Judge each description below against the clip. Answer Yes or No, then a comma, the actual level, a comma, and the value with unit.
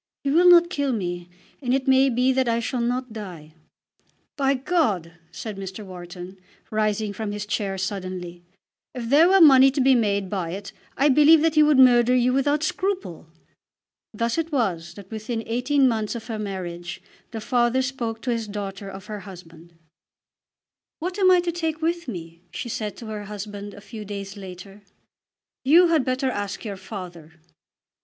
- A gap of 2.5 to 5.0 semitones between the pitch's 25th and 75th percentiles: No, wide, 5.5 semitones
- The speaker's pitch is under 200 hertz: No, high, 225 Hz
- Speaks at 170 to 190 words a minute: Yes, average, 180 wpm